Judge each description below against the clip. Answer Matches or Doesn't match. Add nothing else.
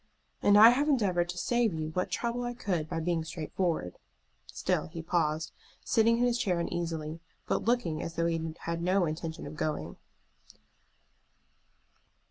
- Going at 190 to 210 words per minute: Doesn't match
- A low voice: Doesn't match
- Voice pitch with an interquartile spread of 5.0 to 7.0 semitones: Matches